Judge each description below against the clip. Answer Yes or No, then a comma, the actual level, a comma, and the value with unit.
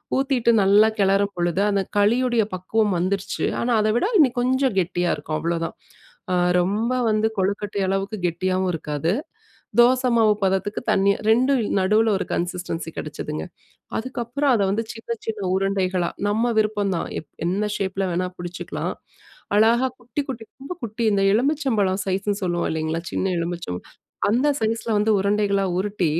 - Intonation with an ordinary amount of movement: Yes, average, 3.7 semitones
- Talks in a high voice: Yes, high, 200 Hz